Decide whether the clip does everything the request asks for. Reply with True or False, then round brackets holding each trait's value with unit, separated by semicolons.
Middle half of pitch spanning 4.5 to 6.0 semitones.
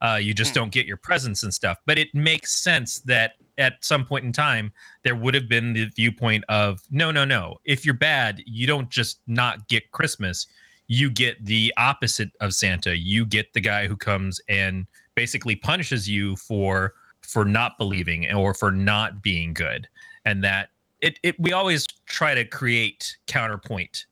True (5.2 semitones)